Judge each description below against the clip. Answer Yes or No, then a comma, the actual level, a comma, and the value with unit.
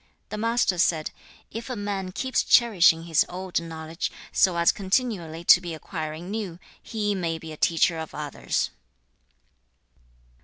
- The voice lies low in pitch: No, medium, 175 Hz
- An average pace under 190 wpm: Yes, average, 145 wpm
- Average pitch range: Yes, average, 4.0 semitones